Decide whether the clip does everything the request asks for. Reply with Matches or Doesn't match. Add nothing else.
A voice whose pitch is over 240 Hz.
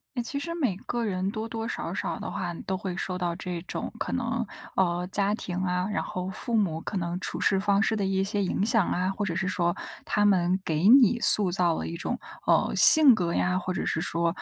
Doesn't match